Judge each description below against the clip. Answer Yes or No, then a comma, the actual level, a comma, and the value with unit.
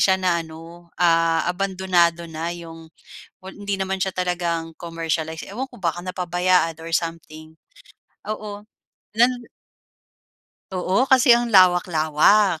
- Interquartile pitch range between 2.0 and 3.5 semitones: Yes, average, 2.7 semitones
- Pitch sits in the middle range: Yes, medium, 175 Hz